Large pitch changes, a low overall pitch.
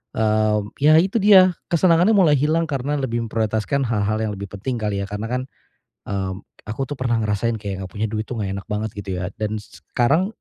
Yes: wide, 5.9 semitones; low, 110 Hz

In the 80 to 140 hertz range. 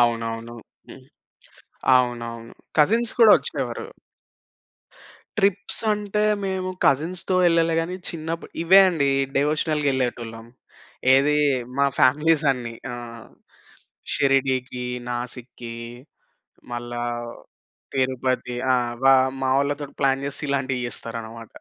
Yes: low, 135 Hz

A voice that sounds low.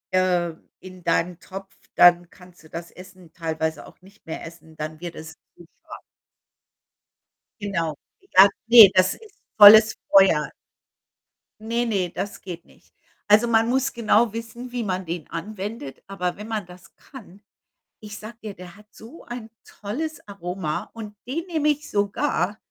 No: high, 195 Hz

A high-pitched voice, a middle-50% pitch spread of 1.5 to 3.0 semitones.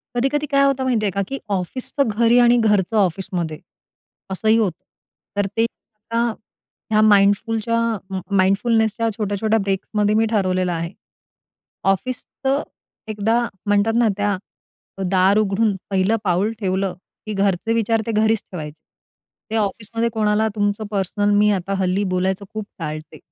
Yes: high, 210 Hz; average, 2.7 semitones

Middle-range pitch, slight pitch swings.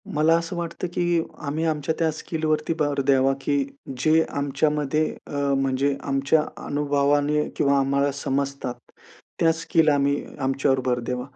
Yes: medium, 145 Hz; narrow, 2.3 semitones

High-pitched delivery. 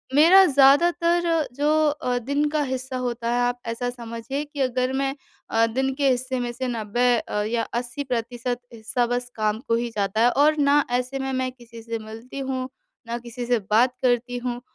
Yes: very high, 250 Hz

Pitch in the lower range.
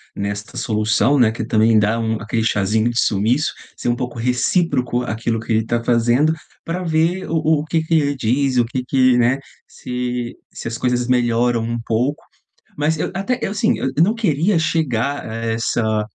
Yes: low, 125 Hz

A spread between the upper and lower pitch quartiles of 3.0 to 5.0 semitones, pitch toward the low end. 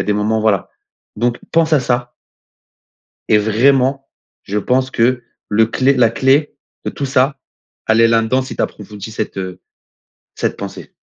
Yes: average, 3.4 semitones; low, 120 Hz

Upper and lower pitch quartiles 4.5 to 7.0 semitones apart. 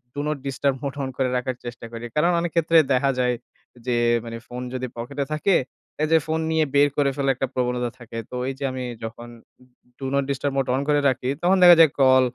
No: average, 2.8 semitones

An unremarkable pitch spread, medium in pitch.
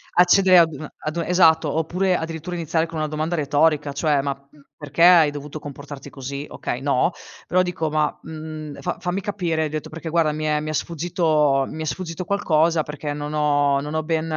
No: narrow, 2.2 semitones; medium, 155 Hz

